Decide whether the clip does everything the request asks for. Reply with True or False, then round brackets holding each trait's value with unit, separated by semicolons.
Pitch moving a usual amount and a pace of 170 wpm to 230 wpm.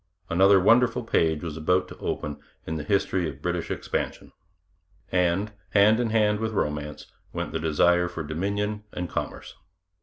False (4.4 semitones; 155 wpm)